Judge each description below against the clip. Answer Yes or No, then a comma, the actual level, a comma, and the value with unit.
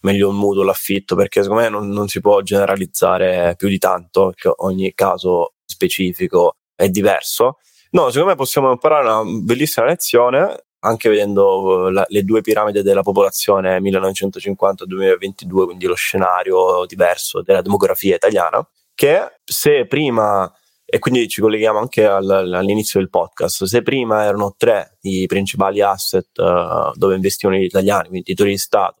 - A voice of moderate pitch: No, low, 100 Hz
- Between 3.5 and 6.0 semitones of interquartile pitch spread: No, average, 2.9 semitones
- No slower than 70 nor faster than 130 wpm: No, average, 150 wpm